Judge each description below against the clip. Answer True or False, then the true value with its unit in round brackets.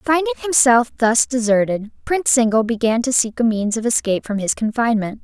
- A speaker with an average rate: True (185 wpm)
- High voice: True (235 Hz)